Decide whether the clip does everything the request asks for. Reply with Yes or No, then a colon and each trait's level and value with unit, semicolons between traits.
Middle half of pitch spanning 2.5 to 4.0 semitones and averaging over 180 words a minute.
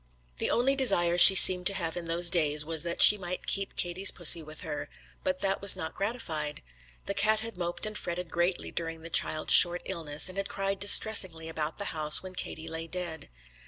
Yes: average, 3.3 semitones; fast, 205 wpm